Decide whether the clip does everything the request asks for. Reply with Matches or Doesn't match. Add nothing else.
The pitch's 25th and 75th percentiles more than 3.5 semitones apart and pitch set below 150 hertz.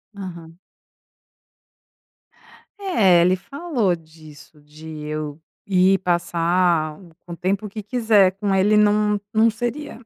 Doesn't match